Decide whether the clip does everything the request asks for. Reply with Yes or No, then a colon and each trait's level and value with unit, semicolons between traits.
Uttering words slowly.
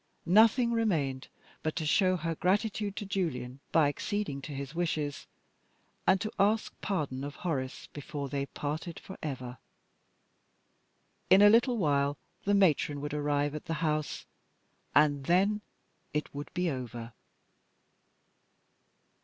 Yes: slow, 130 wpm